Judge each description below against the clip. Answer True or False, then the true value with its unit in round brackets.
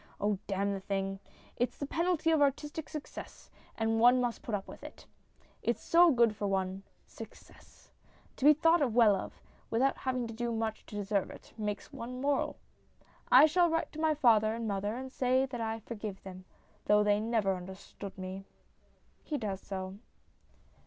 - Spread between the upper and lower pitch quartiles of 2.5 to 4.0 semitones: False (5.0 semitones)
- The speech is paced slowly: False (175 wpm)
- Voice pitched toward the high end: True (225 Hz)